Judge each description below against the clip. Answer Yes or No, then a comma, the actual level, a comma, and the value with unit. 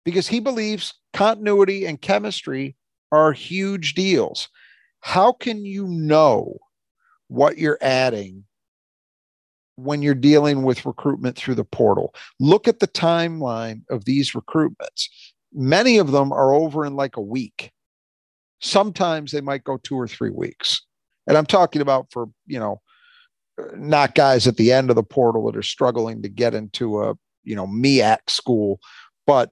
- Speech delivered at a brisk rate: No, average, 150 wpm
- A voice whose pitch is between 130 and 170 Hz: Yes, medium, 140 Hz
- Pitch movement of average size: No, wide, 7.3 semitones